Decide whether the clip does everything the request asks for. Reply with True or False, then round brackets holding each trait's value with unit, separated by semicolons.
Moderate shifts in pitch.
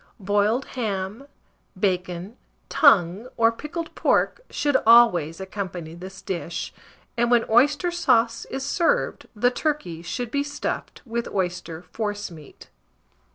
False (6.1 semitones)